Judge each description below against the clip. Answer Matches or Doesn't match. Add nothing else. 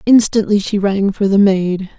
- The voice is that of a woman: Matches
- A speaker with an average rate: Matches